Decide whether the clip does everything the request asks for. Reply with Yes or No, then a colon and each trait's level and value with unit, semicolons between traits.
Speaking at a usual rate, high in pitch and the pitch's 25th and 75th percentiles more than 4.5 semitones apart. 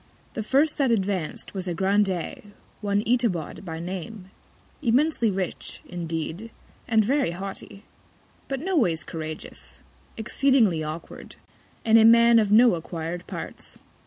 No: slow, 130 wpm; high, 200 Hz; average, 5.2 semitones